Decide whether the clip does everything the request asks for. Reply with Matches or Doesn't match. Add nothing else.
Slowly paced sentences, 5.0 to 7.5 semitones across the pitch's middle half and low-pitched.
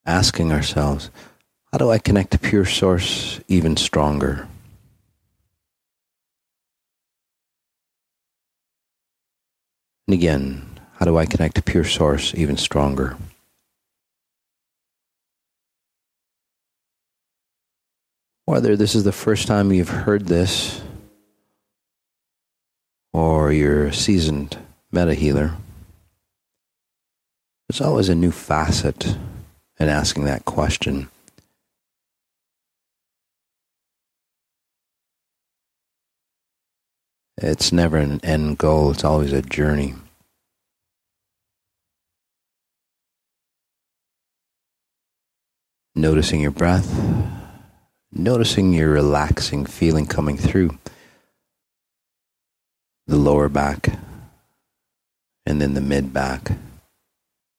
Matches